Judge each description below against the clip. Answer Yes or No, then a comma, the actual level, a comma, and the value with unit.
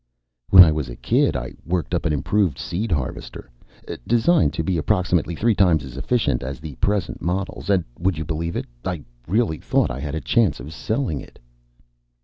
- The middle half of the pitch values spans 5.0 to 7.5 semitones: No, average, 4.5 semitones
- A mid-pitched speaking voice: No, very low, 85 Hz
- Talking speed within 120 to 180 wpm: No, average, 190 wpm